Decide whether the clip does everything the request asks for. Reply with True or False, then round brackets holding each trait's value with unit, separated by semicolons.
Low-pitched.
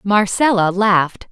False (200 Hz)